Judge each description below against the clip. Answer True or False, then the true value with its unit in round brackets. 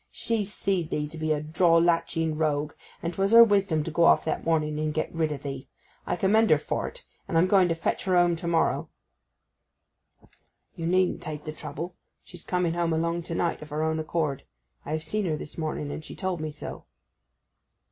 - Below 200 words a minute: False (205 wpm)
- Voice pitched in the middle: True (165 Hz)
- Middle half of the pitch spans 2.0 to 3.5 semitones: True (2.5 semitones)